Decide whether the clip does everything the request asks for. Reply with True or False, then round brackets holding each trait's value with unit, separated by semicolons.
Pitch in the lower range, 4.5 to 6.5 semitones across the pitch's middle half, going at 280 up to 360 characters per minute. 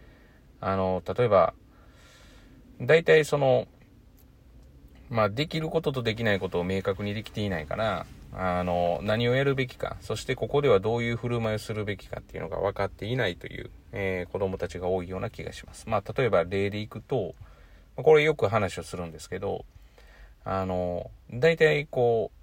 True (105 Hz; 5.1 semitones; 340 characters per minute)